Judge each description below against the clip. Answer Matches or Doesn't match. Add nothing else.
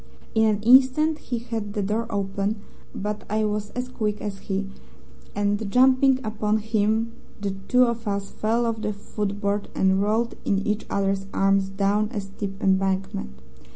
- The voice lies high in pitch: Matches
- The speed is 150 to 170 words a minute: Matches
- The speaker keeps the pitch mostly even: Matches